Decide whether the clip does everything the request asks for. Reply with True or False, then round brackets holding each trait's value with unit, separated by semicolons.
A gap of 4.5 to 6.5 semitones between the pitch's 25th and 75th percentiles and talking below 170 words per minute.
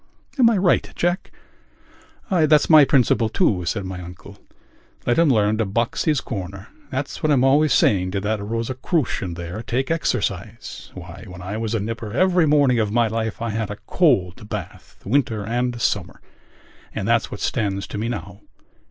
False (4.9 semitones; 175 wpm)